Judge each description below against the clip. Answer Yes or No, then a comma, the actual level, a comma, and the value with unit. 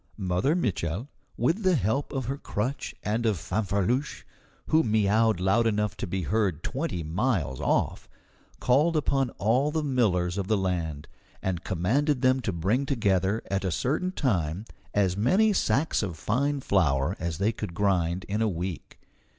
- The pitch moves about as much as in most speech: No, wide, 6.4 semitones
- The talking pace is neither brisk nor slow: Yes, average, 160 wpm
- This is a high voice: No, low, 105 Hz